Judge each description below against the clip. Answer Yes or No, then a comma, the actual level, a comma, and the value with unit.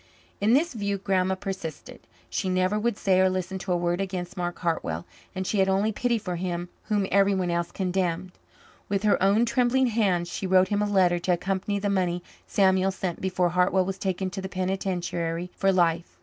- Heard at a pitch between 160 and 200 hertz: Yes, high, 190 Hz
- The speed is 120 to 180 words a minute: No, average, 195 wpm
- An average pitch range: No, narrow, 1.9 semitones